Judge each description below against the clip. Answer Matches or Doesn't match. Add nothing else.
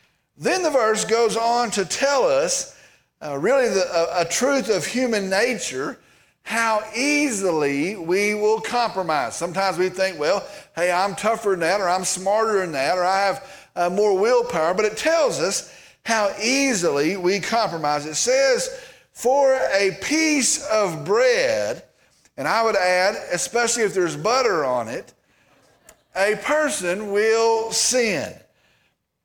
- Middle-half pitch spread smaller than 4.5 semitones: Doesn't match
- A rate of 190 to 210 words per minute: Doesn't match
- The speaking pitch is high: Matches